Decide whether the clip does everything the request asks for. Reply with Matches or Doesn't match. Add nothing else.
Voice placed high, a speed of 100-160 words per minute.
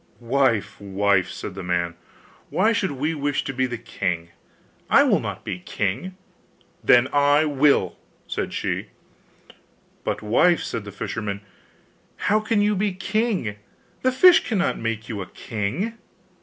Doesn't match